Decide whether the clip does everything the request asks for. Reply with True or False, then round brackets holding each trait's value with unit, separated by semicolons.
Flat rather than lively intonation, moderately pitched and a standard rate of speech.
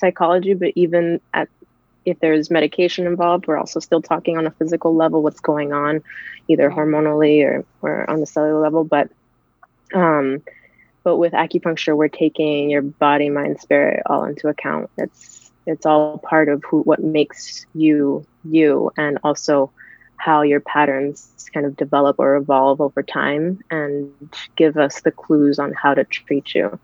True (1.8 semitones; 155 Hz; 165 wpm)